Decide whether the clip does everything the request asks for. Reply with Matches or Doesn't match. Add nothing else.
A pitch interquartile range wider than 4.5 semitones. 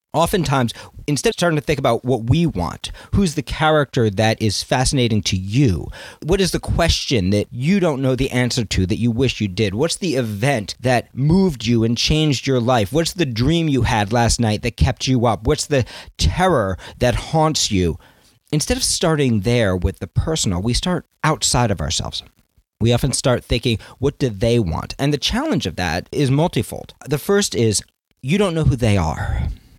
Matches